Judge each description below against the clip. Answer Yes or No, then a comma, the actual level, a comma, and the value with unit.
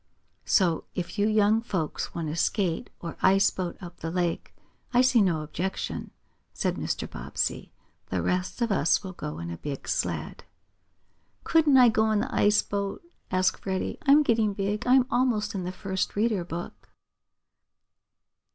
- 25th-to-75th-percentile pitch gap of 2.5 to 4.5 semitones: Yes, average, 4.0 semitones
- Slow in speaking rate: No, average, 160 wpm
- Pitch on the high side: Yes, high, 195 Hz